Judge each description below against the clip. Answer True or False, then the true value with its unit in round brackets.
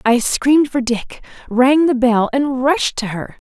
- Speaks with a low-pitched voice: False (255 Hz)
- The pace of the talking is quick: False (190 wpm)